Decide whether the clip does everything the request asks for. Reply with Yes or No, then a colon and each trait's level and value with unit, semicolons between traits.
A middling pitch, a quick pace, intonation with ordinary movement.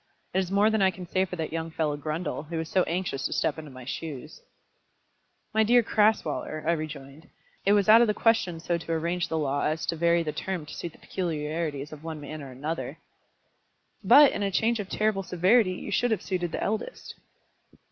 Yes: medium, 170 Hz; fast, 220 wpm; average, 4.1 semitones